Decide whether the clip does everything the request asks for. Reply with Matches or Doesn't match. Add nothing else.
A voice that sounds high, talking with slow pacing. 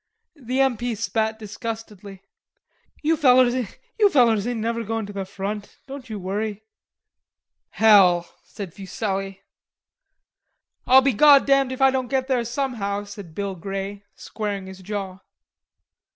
Matches